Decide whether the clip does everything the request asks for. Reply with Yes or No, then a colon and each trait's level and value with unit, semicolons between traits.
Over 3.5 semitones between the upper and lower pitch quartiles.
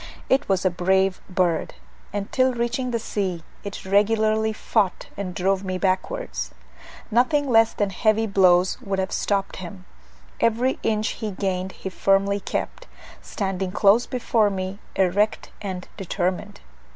No: average, 2.7 semitones